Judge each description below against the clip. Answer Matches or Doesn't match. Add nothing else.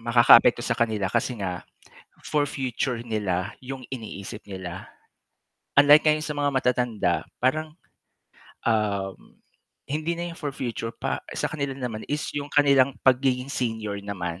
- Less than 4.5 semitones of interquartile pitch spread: Doesn't match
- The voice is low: Matches